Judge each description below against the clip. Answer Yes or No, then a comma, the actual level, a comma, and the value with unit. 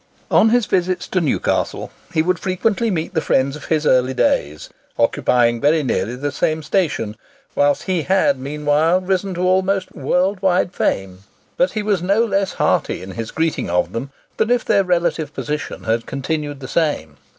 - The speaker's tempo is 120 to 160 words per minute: No, average, 175 wpm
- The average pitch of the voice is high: No, medium, 160 Hz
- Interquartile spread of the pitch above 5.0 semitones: Yes, wide, 5.5 semitones